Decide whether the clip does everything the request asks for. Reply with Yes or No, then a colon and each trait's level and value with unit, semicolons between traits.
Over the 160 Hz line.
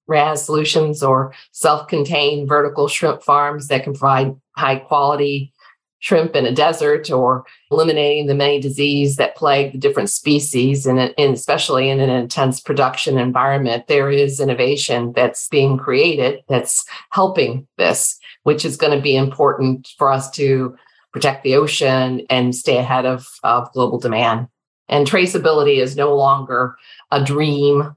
No: medium, 140 Hz